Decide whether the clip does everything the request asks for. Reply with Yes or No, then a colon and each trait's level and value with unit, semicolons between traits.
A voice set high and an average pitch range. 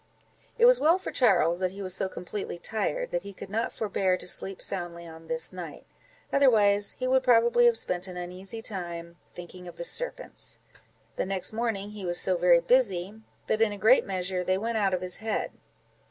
Yes: high, 195 Hz; average, 4.0 semitones